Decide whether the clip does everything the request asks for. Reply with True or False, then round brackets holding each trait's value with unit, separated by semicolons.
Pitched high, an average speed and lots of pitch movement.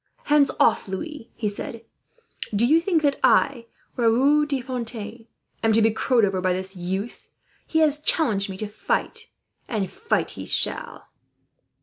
True (230 Hz; 155 wpm; 6.1 semitones)